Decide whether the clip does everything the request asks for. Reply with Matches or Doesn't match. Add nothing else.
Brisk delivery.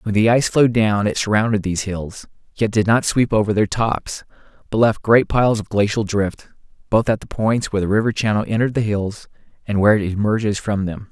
Matches